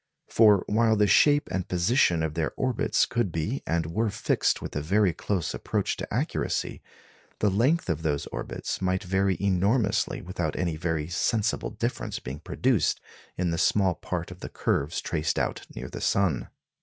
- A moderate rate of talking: Yes, average, 170 wpm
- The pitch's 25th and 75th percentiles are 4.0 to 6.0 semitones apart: Yes, average, 4.3 semitones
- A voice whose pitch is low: Yes, very low, 95 Hz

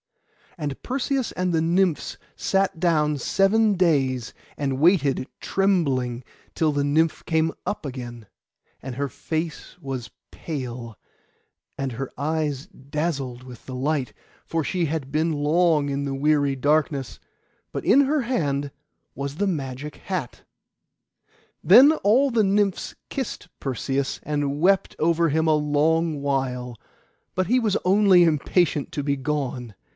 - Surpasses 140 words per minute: No, slow, 135 wpm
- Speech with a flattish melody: No, average, 4.6 semitones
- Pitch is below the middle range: No, medium, 150 Hz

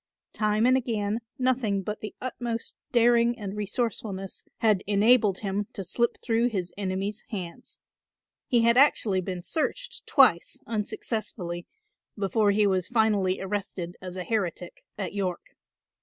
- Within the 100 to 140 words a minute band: Yes, slow, 135 wpm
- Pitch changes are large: No, average, 3.5 semitones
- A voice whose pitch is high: Yes, high, 210 Hz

